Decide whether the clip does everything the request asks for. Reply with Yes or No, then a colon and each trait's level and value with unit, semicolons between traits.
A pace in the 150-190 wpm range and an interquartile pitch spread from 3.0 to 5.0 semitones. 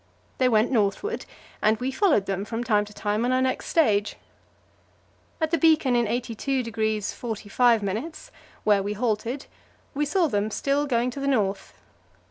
Yes: average, 155 wpm; average, 4.6 semitones